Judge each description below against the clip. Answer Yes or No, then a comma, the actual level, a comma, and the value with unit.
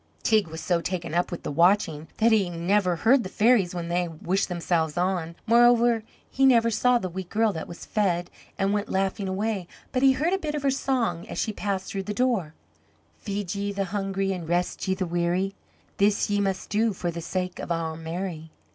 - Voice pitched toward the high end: Yes, high, 195 Hz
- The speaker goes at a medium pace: No, fast, 210 wpm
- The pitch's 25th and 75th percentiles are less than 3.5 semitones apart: No, average, 3.8 semitones